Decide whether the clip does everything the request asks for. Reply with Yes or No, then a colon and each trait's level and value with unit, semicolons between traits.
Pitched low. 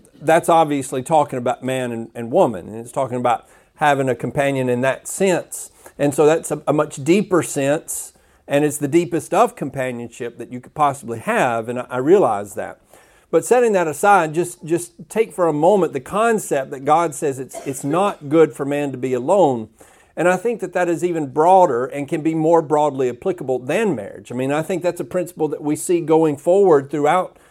No: medium, 150 Hz